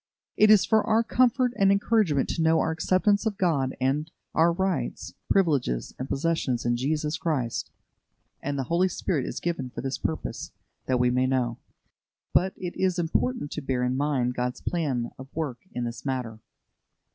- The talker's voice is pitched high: No, medium, 150 Hz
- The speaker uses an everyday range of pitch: No, wide, 6.2 semitones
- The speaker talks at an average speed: Yes, average, 175 wpm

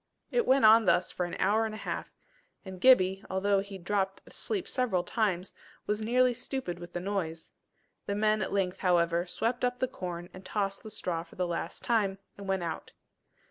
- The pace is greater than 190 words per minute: Yes, average, 200 wpm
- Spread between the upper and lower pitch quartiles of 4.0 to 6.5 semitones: No, average, 3.5 semitones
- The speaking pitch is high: Yes, high, 195 Hz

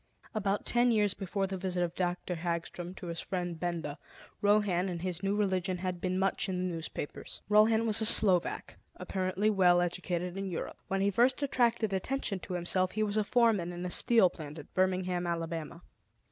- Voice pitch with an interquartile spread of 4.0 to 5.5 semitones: No, average, 2.7 semitones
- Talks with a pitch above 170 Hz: Yes, medium, 185 Hz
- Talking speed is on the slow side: No, average, 185 wpm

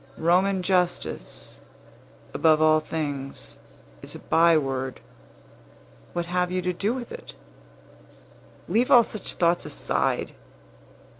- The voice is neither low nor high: Yes, medium, 175 Hz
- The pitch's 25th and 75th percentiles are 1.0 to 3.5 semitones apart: Yes, average, 2.8 semitones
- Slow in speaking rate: Yes, slow, 105 wpm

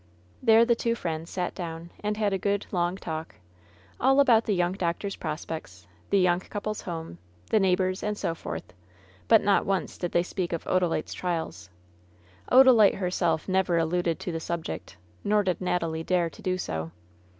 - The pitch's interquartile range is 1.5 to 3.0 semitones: No, average, 3.6 semitones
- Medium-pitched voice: Yes, medium, 180 Hz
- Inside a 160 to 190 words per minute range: Yes, average, 175 wpm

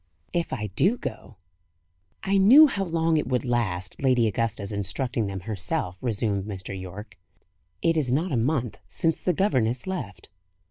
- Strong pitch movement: Yes, wide, 7.8 semitones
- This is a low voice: Yes, low, 120 Hz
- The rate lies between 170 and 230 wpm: No, average, 155 wpm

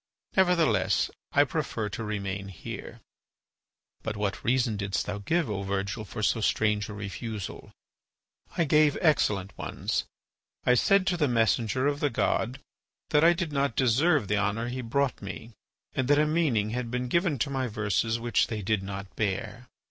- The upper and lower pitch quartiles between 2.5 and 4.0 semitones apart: No, wide, 5.4 semitones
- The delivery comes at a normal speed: Yes, average, 170 wpm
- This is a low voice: Yes, low, 115 Hz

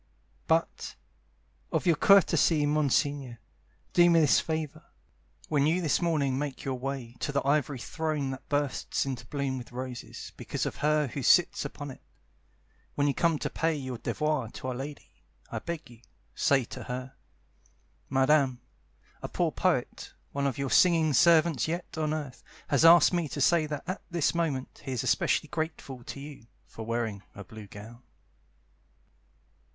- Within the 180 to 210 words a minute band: No, average, 165 wpm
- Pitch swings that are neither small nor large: Yes, average, 3.3 semitones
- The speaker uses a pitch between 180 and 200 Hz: No, medium, 145 Hz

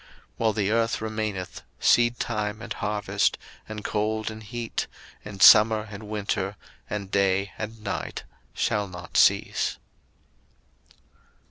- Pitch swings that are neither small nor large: No, narrow, 1.5 semitones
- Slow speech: Yes, slow, 120 wpm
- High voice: No, low, 105 Hz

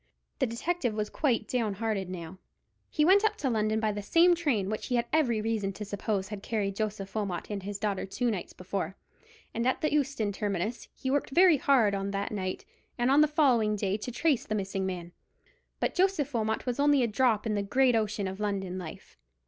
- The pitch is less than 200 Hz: No, high, 215 Hz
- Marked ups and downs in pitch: No, average, 4.7 semitones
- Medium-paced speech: No, fast, 215 wpm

